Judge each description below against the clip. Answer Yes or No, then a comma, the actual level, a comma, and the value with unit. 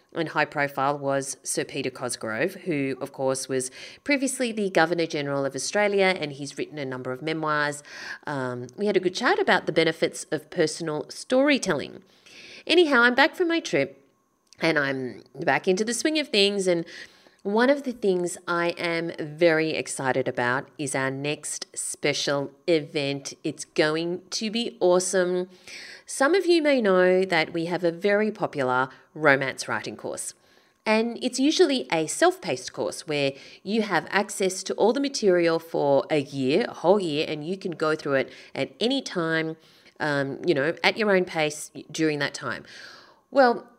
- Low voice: No, medium, 165 Hz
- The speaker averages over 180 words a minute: No, average, 170 wpm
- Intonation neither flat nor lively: No, wide, 5.8 semitones